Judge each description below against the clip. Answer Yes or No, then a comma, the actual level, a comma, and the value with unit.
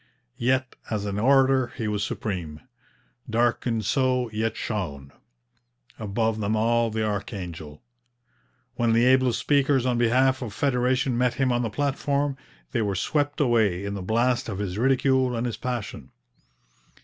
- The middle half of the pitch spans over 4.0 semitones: No, average, 3.7 semitones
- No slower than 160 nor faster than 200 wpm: No, average, 150 wpm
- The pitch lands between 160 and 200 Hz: No, low, 120 Hz